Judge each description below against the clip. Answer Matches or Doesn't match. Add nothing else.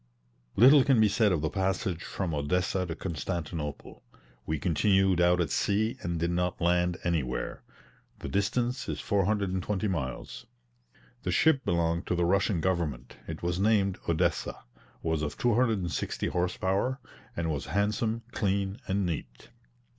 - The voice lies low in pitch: Matches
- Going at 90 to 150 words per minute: Matches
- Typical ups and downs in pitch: Matches